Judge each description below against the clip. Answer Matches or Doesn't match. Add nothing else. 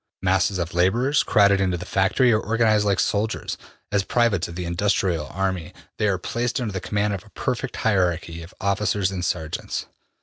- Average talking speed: Matches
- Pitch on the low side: Matches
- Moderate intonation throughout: Matches